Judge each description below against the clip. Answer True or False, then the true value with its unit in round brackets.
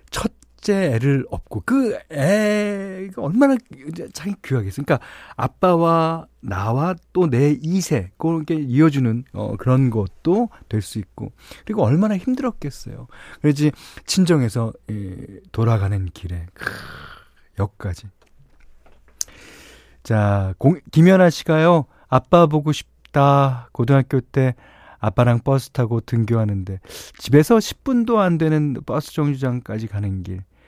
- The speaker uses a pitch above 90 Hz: True (135 Hz)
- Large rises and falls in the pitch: True (7.0 semitones)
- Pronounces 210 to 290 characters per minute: True (235 characters per minute)